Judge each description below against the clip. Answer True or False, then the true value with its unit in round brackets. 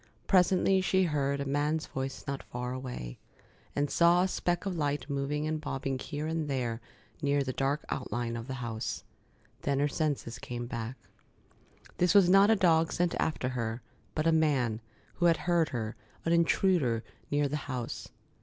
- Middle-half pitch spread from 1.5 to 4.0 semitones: False (4.5 semitones)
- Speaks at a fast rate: False (175 wpm)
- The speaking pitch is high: False (145 Hz)